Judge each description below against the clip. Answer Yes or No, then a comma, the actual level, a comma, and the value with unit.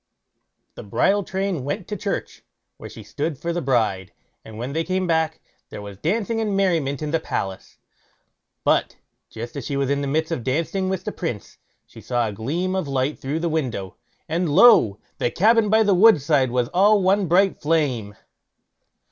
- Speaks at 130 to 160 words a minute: No, average, 190 wpm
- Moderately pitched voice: Yes, medium, 160 Hz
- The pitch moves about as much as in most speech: No, wide, 6.6 semitones